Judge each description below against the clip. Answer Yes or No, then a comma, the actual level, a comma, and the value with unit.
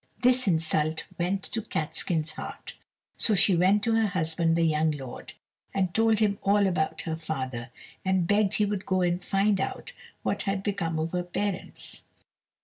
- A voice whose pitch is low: No, medium, 180 Hz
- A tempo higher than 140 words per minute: Yes, average, 170 wpm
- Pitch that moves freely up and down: No, average, 3.9 semitones